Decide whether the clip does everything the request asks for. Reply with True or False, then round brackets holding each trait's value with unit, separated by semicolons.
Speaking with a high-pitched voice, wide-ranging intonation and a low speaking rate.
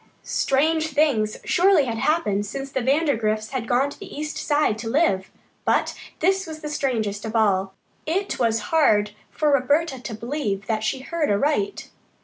False (270 Hz; 6.1 semitones; 165 wpm)